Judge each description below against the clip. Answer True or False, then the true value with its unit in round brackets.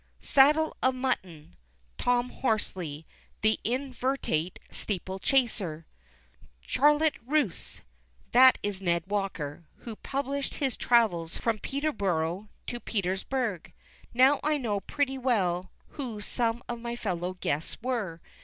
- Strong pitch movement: True (6.1 semitones)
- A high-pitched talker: True (230 Hz)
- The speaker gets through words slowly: True (115 wpm)